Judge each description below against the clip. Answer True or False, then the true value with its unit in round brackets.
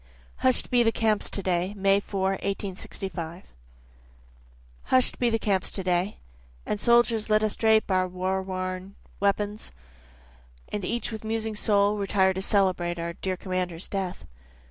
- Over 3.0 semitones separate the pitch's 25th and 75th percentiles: False (2.5 semitones)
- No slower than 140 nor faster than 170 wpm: True (145 wpm)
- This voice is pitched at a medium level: False (195 Hz)